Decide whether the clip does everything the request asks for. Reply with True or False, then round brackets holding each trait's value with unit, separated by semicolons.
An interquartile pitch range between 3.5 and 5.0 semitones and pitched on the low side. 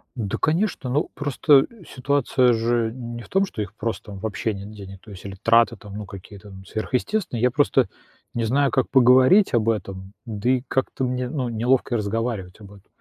True (3.8 semitones; 115 Hz)